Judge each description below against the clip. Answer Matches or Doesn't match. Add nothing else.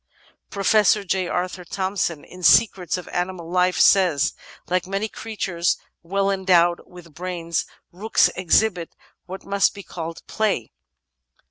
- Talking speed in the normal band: Doesn't match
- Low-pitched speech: Doesn't match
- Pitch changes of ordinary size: Doesn't match